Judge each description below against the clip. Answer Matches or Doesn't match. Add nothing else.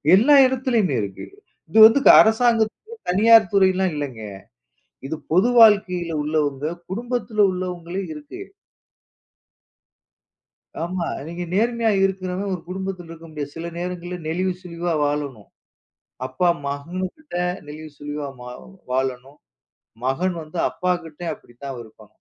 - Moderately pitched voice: Matches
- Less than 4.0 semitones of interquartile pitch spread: Doesn't match